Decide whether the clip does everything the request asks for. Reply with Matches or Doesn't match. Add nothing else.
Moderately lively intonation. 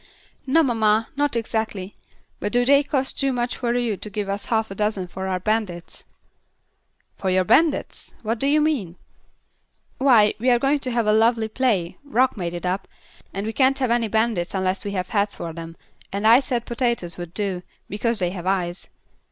Matches